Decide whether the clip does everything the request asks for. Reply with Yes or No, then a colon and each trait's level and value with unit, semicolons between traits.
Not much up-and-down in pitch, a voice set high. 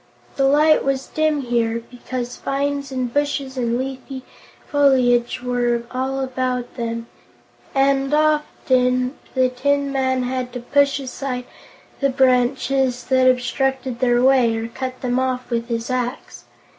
Yes: narrow, 1.7 semitones; very high, 255 Hz